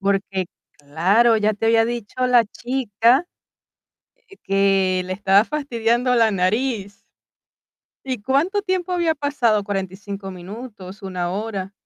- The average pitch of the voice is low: No, high, 215 Hz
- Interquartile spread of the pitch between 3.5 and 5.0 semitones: Yes, average, 4.4 semitones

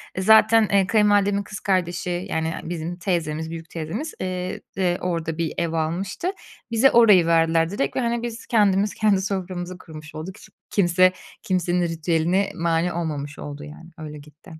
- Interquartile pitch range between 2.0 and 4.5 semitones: Yes, average, 3.3 semitones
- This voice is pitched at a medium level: Yes, medium, 175 Hz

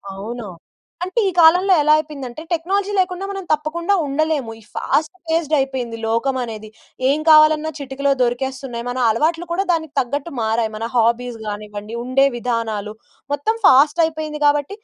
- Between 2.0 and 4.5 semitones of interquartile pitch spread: No, average, 5.1 semitones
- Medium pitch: No, very high, 280 Hz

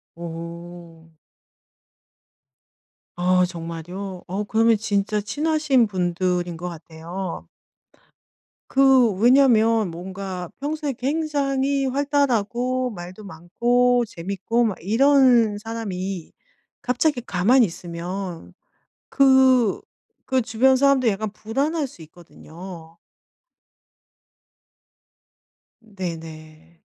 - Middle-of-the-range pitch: No, high, 210 Hz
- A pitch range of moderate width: No, wide, 6.5 semitones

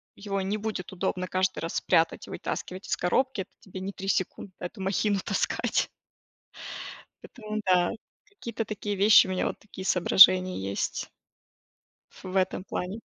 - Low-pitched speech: No, high, 190 Hz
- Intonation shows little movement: Yes, narrow, 2.0 semitones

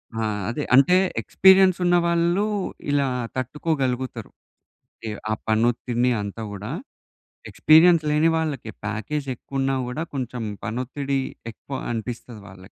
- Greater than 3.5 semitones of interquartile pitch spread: Yes, average, 5.3 semitones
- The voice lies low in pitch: Yes, low, 130 Hz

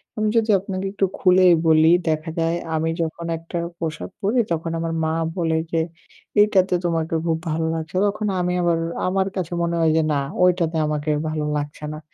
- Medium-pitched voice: Yes, medium, 165 Hz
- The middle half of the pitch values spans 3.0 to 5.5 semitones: No, narrow, 2.4 semitones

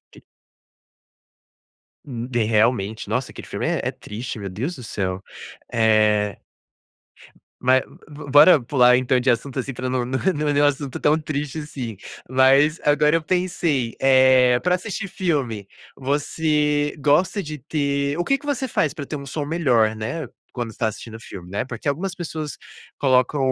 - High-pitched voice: No, low, 135 Hz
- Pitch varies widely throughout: No, average, 3.9 semitones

